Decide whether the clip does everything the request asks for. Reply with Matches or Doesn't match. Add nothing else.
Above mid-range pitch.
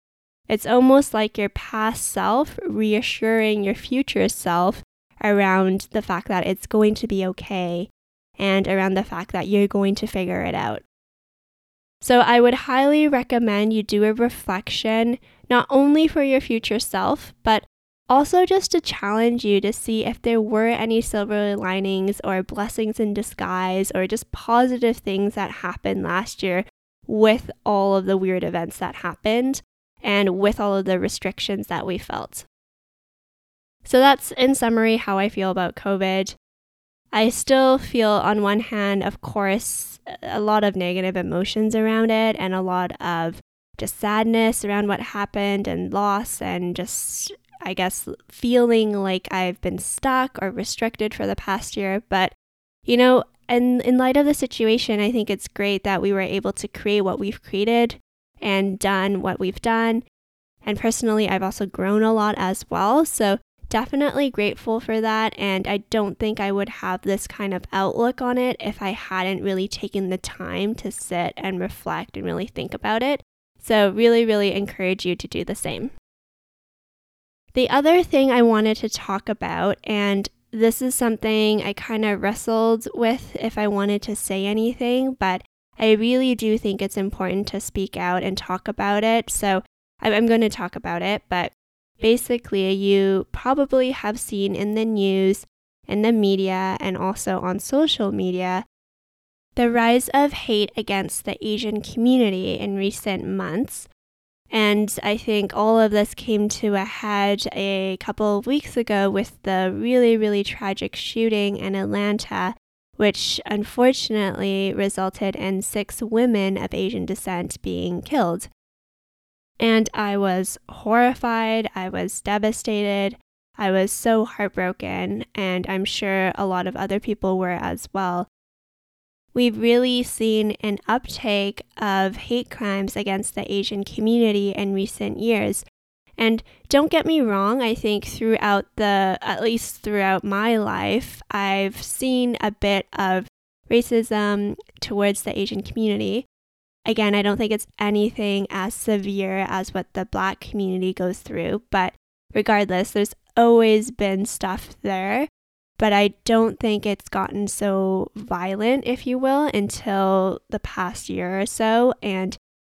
Matches